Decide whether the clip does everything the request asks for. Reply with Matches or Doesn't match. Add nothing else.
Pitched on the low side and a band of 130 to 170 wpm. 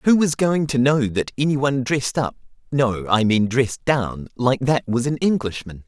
Doesn't match